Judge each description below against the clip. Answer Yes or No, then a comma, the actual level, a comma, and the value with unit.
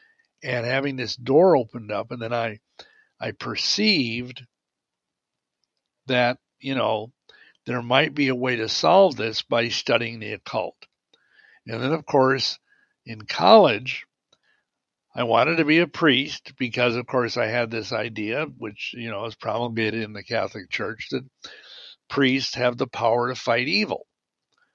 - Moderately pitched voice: No, low, 125 Hz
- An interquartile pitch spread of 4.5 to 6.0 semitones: No, average, 2.8 semitones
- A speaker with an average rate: Yes, average, 150 wpm